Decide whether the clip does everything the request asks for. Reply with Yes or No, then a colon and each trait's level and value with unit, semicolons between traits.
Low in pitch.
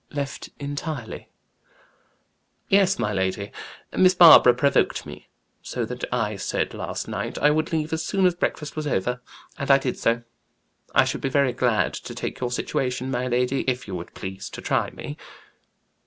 Yes: low, 130 Hz